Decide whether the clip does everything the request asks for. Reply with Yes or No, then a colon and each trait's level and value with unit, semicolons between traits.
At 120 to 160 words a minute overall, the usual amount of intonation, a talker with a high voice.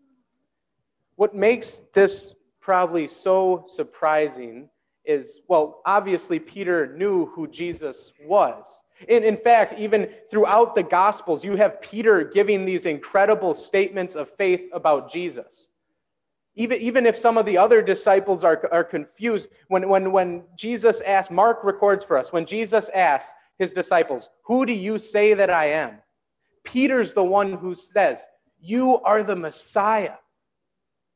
Yes: average, 140 wpm; average, 3.9 semitones; high, 205 Hz